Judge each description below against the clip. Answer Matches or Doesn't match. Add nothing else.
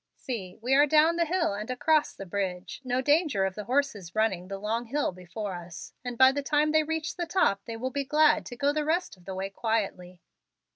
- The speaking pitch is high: Matches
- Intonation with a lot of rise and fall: Matches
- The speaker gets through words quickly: Matches